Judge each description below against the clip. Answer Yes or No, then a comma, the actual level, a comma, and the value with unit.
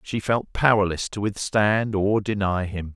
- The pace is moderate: Yes, average, 165 wpm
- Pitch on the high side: No, low, 100 Hz